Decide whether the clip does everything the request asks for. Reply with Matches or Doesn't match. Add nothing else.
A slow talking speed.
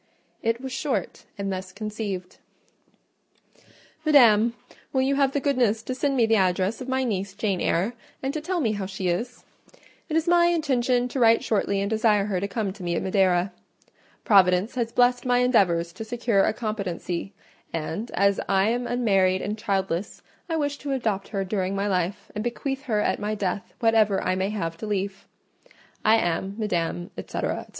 Doesn't match